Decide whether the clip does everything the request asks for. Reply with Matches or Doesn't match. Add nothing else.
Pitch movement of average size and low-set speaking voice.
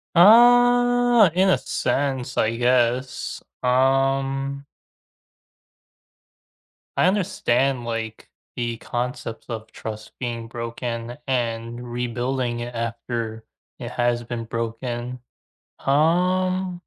Matches